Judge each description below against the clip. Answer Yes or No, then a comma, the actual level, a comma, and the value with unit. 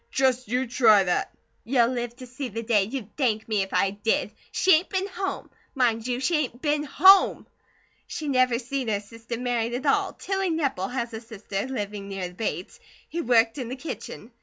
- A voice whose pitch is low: No, high, 245 Hz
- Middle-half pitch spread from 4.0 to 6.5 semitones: No, average, 3.6 semitones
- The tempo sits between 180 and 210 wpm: Yes, average, 200 wpm